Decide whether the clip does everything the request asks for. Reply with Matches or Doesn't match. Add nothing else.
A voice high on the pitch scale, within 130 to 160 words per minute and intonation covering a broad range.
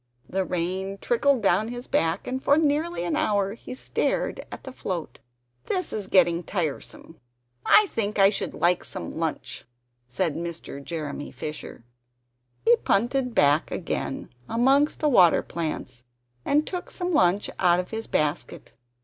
Matches